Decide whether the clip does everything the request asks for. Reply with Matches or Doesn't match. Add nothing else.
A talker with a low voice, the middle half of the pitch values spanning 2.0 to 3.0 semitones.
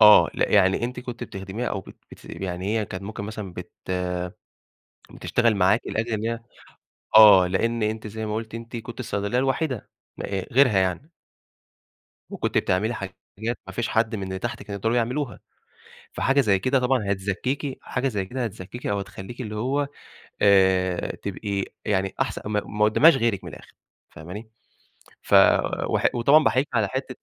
Doesn't match